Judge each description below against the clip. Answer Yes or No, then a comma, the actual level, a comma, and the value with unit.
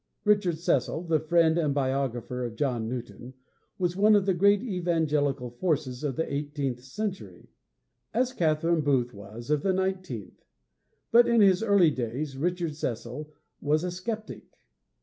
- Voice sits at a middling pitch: Yes, medium, 155 Hz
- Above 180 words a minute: No, average, 150 wpm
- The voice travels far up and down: Yes, wide, 6.0 semitones